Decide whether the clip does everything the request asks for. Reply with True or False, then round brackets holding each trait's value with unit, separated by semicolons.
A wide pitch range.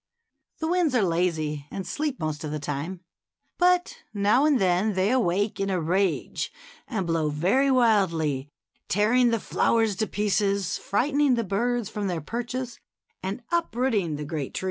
True (6.3 semitones)